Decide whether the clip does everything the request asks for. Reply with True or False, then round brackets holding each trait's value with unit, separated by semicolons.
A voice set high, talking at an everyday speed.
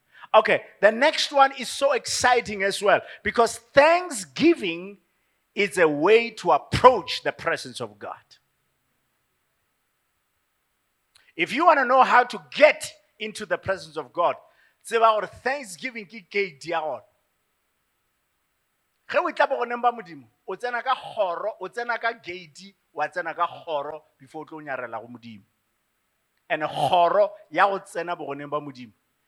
False (210 Hz; 100 wpm)